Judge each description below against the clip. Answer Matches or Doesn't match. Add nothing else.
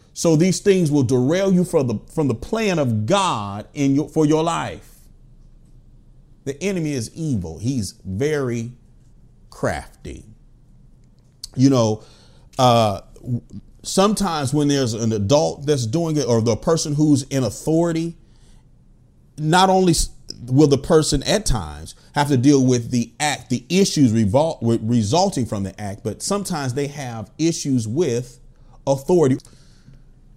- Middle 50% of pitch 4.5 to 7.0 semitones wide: Matches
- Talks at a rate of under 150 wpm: Matches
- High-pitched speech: Doesn't match